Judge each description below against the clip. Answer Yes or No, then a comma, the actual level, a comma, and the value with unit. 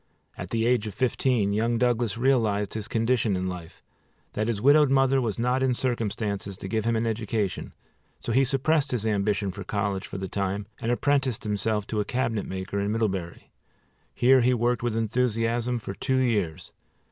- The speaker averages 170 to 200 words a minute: Yes, average, 180 wpm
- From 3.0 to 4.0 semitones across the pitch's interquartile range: Yes, average, 3.4 semitones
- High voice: No, low, 115 Hz